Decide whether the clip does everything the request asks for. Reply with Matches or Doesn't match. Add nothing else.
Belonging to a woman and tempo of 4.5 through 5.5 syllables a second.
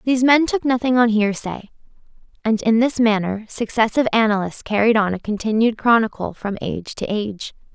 Doesn't match